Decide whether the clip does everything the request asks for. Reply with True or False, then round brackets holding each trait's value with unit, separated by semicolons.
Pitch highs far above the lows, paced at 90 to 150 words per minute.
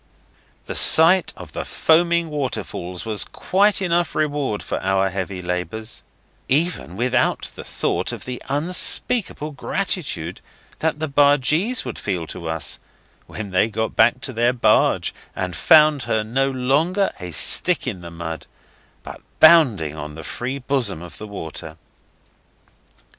True (8.5 semitones; 140 wpm)